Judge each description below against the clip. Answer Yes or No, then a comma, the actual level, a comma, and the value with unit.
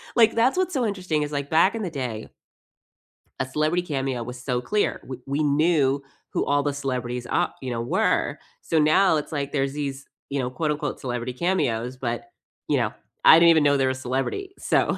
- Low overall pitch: No, medium, 145 Hz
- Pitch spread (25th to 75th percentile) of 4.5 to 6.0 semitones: No, average, 4.0 semitones